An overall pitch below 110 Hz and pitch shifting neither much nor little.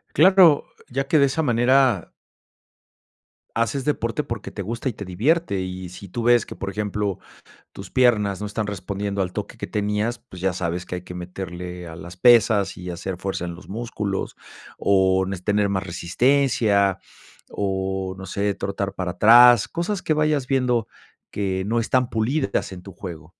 Yes: low, 100 Hz; average, 4.4 semitones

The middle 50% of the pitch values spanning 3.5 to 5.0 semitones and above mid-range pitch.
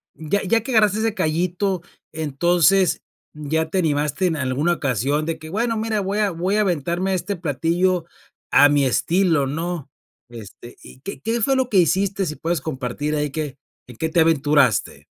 No: average, 4.6 semitones; medium, 165 Hz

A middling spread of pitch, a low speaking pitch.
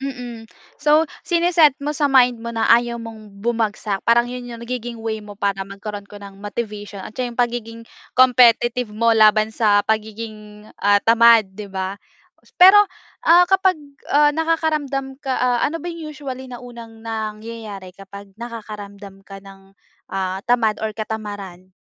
No: average, 3.3 semitones; high, 225 Hz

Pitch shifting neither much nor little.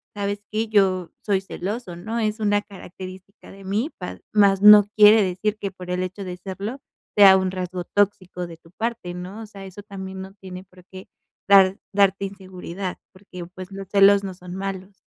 No: narrow, 1.8 semitones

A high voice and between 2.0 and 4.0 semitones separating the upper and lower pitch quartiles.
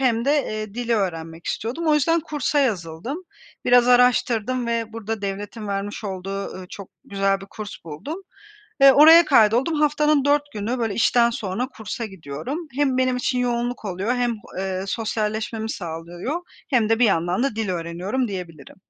No: high, 225 Hz; average, 4.7 semitones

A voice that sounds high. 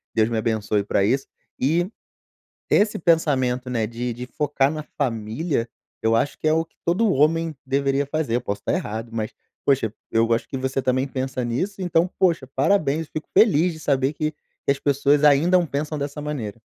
No: medium, 140 Hz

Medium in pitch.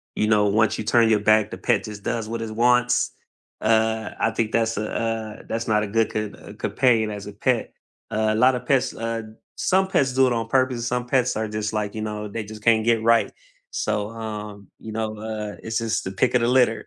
No: low, 110 Hz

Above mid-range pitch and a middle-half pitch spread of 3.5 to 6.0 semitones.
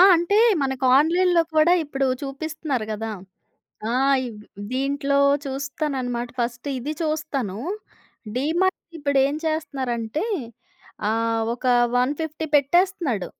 Yes: very high, 280 Hz; average, 4.1 semitones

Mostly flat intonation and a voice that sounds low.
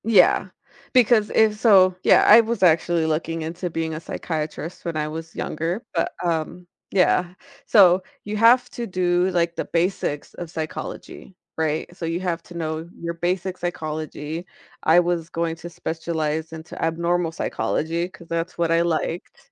No: narrow, 2.1 semitones; medium, 170 Hz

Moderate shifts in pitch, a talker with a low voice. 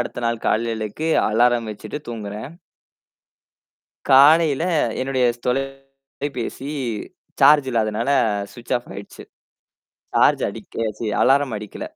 Yes: average, 3.3 semitones; low, 125 Hz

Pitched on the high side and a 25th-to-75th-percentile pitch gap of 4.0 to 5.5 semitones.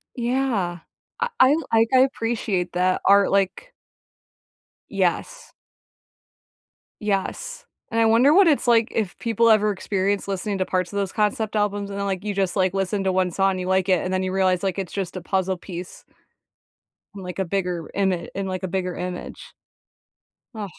No: high, 195 Hz; average, 2.9 semitones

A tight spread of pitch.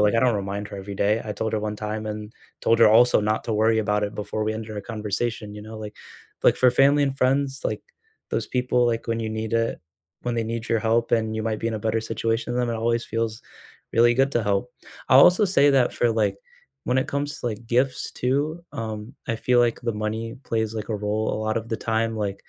Yes: narrow, 2.1 semitones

